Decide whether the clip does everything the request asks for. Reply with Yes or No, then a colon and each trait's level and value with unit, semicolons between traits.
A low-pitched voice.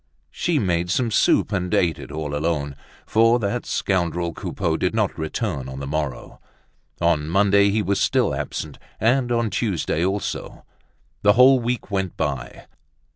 Yes: very low, 95 Hz